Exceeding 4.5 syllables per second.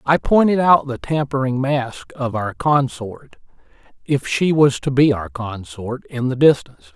No: 4.4 syllables/s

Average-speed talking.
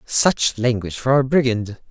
Yes: average, 155 wpm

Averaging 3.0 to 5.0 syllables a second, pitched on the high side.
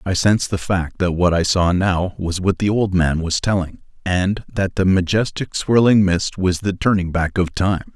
No: 4.5 syllables/s; very low, 95 Hz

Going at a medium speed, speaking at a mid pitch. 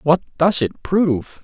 Yes: average, 165 wpm; medium, 160 Hz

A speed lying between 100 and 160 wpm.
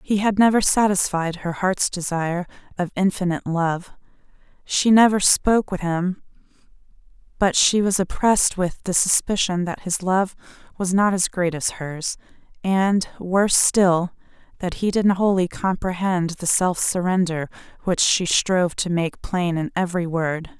Yes: average, 150 wpm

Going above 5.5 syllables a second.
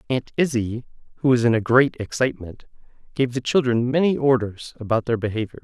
Yes: 5.8 syllables/s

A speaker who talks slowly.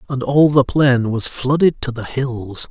No: average, 200 wpm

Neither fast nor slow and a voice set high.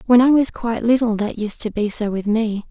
No: fast, 265 wpm; high, 225 Hz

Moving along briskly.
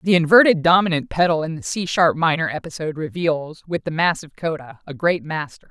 No: average, 190 wpm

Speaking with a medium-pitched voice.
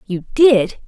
No: high, 220 Hz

